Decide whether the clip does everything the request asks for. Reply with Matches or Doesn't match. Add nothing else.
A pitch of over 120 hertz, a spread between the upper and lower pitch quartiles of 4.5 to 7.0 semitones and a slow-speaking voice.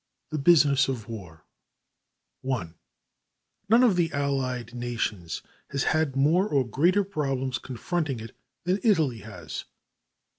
Matches